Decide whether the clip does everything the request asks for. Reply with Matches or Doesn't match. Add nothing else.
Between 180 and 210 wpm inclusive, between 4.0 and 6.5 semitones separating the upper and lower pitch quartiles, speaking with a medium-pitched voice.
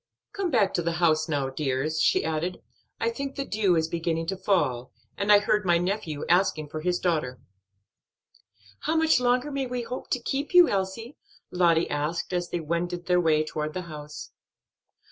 Matches